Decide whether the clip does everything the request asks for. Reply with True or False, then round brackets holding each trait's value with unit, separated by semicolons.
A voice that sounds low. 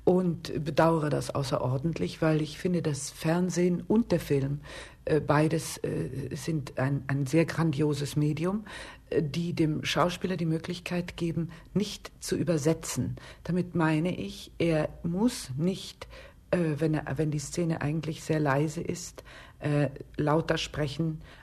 False (160 Hz)